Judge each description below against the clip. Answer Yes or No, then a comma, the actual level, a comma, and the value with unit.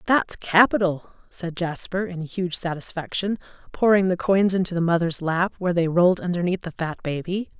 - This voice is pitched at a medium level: Yes, medium, 180 Hz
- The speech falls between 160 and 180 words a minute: Yes, average, 165 wpm